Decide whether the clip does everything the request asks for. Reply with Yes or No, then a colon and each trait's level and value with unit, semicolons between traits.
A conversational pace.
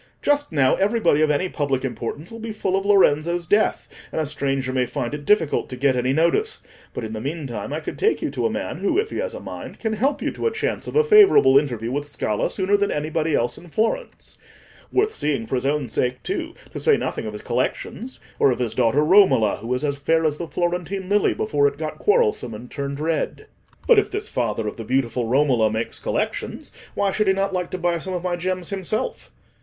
No: fast, 230 wpm